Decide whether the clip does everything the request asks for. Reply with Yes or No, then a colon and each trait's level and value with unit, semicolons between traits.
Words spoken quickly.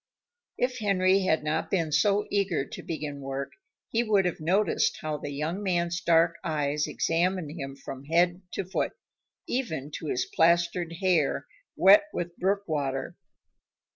No: average, 150 wpm